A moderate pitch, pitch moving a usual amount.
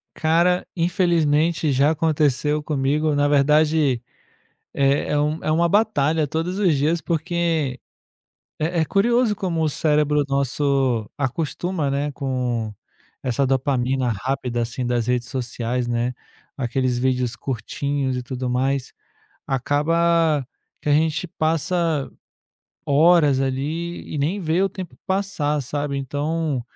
Yes: medium, 145 Hz; average, 3.7 semitones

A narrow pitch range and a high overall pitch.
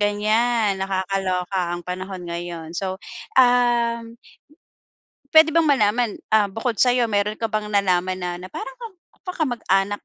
No: average, 4.1 semitones; high, 205 Hz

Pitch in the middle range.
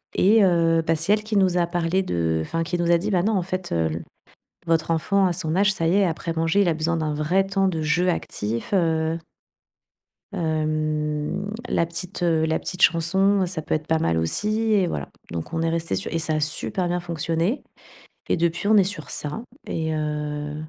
Yes: medium, 165 Hz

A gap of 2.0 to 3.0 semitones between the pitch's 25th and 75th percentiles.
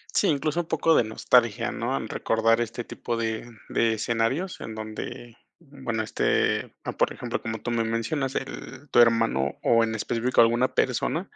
Yes: narrow, 2.6 semitones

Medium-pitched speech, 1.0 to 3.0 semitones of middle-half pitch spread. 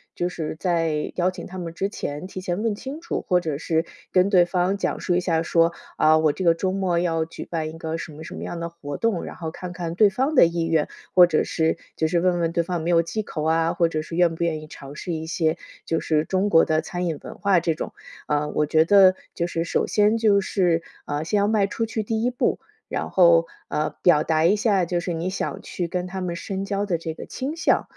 Yes: medium, 170 Hz; narrow, 2.6 semitones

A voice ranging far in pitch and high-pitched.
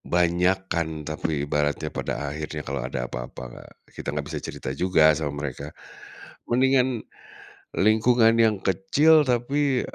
No: wide, 8.3 semitones; very low, 90 Hz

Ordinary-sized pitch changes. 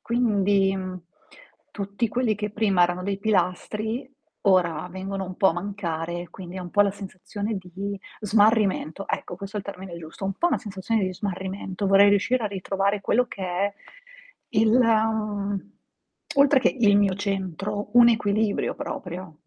No: narrow, 2.2 semitones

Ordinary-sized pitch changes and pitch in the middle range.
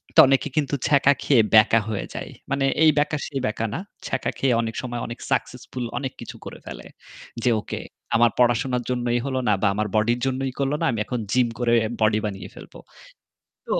No: average, 3.0 semitones; low, 125 Hz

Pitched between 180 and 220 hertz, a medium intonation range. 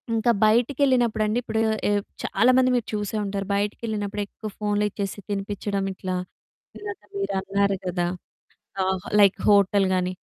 No: high, 205 Hz; narrow, 2.2 semitones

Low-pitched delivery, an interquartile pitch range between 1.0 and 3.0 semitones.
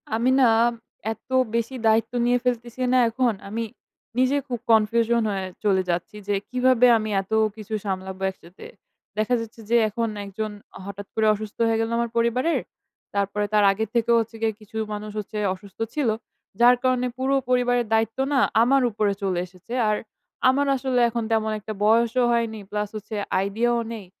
No: high, 225 Hz; narrow, 2.6 semitones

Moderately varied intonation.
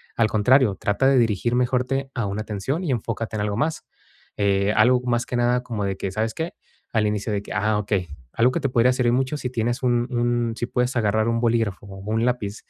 Yes: average, 3.0 semitones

